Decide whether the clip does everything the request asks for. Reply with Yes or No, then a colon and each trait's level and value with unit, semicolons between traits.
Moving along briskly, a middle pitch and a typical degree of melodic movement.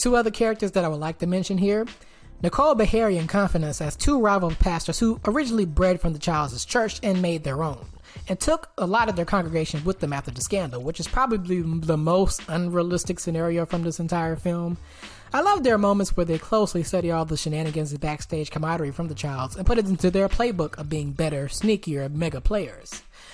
Yes: fast, 210 wpm; medium, 170 Hz; average, 4.1 semitones